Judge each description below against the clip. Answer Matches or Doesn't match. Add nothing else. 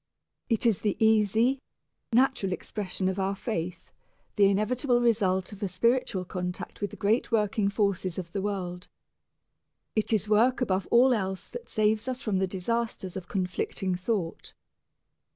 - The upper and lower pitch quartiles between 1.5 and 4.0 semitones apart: Matches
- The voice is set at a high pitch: Matches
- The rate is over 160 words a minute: Doesn't match